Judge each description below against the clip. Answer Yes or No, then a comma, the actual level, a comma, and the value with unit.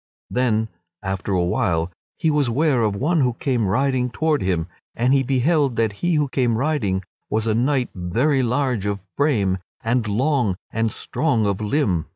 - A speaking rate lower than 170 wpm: No, average, 175 wpm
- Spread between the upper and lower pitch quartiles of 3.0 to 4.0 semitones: No, wide, 5.4 semitones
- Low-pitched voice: Yes, low, 120 Hz